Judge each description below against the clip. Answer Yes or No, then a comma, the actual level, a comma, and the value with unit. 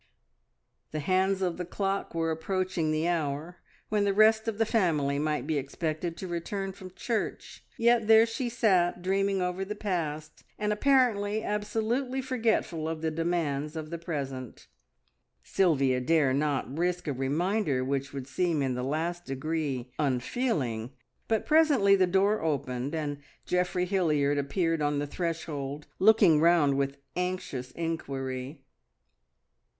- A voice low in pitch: No, medium, 170 Hz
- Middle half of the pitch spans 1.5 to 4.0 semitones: No, average, 5.3 semitones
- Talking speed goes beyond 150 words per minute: No, average, 145 wpm